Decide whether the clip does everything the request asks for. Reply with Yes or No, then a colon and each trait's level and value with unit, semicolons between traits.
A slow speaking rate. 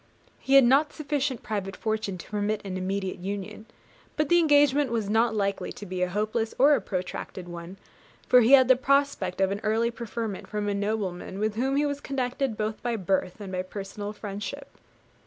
No: average, 190 wpm